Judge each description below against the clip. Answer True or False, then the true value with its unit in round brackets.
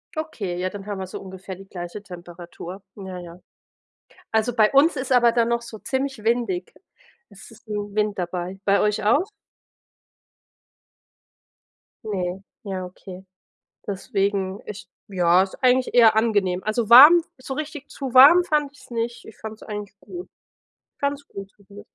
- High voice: True (210 Hz)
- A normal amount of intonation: True (4.4 semitones)